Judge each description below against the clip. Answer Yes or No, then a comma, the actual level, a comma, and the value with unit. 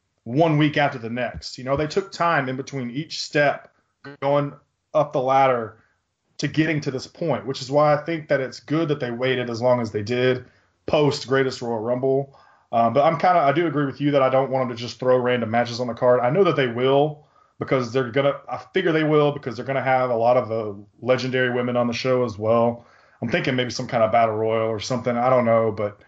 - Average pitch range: Yes, average, 3.1 semitones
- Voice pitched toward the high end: No, low, 130 Hz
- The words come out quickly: Yes, fast, 250 wpm